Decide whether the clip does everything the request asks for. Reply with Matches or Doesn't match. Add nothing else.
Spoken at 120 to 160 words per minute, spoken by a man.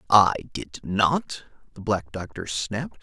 Matches